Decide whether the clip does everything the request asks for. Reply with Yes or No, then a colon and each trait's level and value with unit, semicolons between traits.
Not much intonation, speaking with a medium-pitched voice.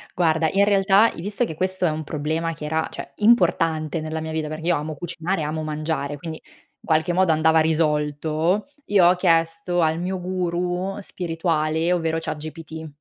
Yes: narrow, 2.3 semitones; medium, 165 Hz